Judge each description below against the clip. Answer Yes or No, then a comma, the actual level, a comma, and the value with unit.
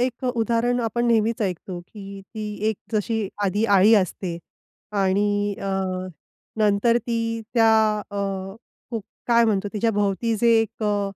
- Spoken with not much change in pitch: Yes, narrow, 2.3 semitones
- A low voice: No, high, 215 Hz